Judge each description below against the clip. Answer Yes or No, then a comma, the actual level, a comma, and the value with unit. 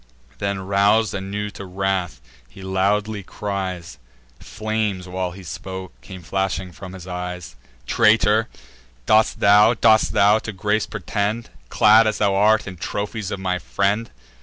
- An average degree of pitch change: No, narrow, 2.2 semitones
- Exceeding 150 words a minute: No, average, 140 wpm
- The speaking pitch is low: Yes, low, 100 Hz